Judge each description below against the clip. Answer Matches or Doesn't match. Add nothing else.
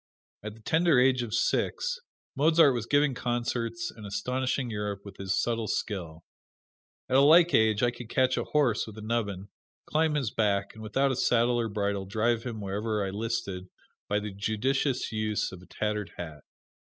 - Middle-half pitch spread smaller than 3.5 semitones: Doesn't match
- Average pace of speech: Matches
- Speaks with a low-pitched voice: Matches